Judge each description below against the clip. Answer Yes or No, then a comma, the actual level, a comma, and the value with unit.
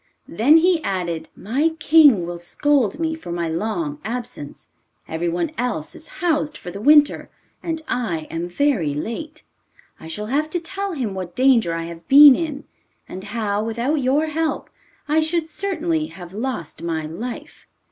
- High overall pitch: Yes, very high, 250 Hz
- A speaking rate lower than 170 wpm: Yes, average, 160 wpm